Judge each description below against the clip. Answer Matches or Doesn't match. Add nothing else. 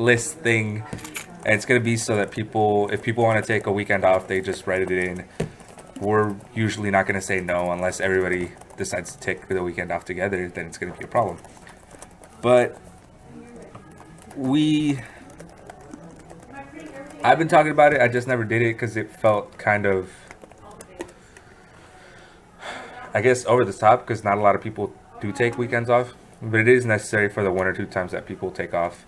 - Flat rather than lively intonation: Doesn't match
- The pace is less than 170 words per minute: Doesn't match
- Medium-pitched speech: Doesn't match